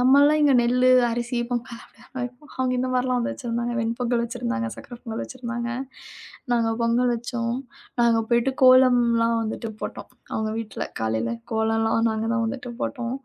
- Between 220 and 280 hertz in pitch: Yes, high, 240 Hz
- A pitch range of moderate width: No, narrow, 1.6 semitones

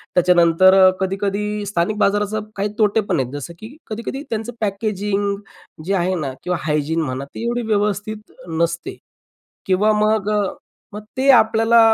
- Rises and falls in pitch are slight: No, average, 3.4 semitones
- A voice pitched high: Yes, high, 205 Hz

